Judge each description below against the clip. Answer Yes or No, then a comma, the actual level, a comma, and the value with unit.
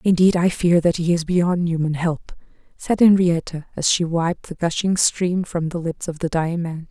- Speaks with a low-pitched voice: No, medium, 170 Hz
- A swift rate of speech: Yes, fast, 210 wpm